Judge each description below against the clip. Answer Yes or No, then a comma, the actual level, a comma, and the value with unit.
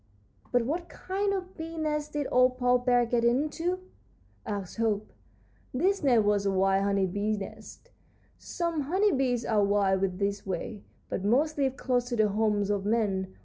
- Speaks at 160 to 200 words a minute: Yes, average, 170 wpm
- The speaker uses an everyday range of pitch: No, wide, 6.5 semitones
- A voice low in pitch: No, high, 235 Hz